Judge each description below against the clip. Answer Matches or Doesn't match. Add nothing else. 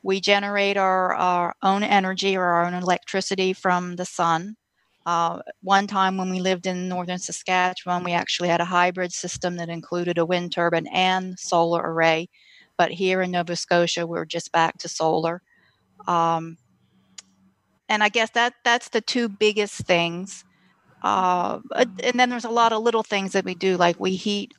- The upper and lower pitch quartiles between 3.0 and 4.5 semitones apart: Doesn't match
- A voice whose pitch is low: Doesn't match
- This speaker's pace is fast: Doesn't match